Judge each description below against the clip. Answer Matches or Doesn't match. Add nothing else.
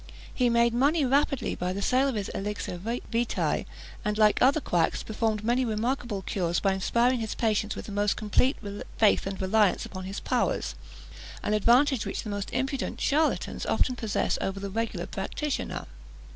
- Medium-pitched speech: Doesn't match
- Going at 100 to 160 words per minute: Doesn't match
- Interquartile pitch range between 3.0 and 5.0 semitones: Matches